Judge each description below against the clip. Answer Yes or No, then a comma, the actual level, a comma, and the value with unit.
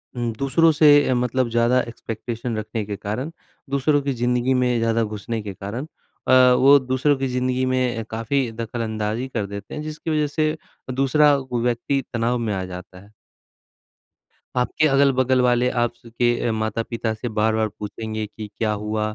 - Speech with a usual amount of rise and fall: Yes, average, 3.0 semitones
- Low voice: Yes, low, 120 Hz